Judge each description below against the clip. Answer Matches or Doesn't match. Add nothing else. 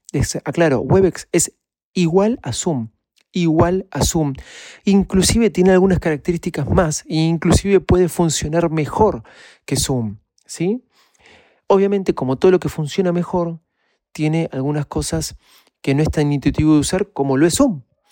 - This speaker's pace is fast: Doesn't match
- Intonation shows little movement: Doesn't match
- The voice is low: Doesn't match